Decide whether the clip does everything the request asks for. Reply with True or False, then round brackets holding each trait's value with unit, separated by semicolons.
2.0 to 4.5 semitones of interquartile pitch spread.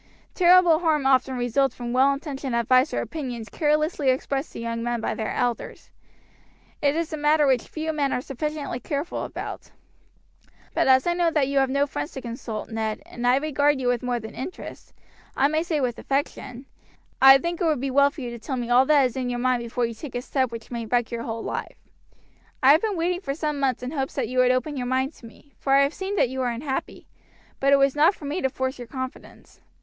True (3.3 semitones)